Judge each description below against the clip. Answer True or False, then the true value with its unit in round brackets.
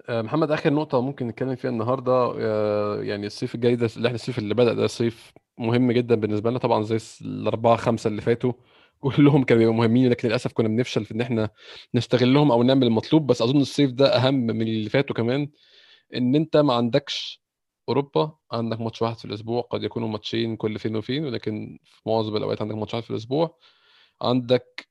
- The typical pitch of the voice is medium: False (120 Hz)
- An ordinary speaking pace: False (185 wpm)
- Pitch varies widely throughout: False (2.5 semitones)